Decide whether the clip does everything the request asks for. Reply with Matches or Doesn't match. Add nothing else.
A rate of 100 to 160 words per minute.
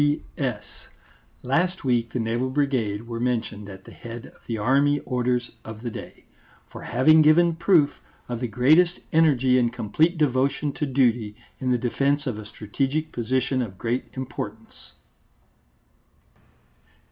Matches